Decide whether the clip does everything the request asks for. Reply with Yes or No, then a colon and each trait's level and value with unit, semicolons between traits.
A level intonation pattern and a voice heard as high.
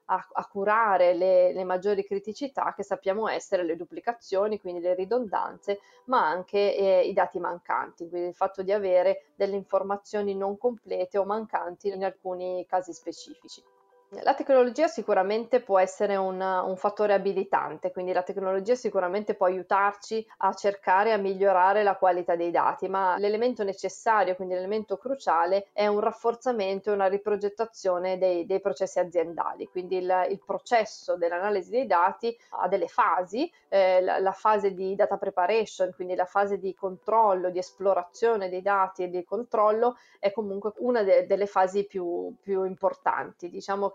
Yes: narrow, 2.3 semitones; high, 195 Hz